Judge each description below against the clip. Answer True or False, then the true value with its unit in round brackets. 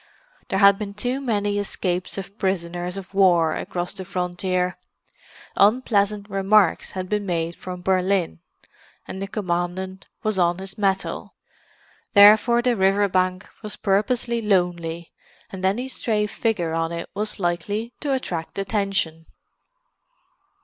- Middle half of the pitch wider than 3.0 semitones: False (2.6 semitones)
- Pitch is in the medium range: False (195 Hz)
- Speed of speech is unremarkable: False (130 wpm)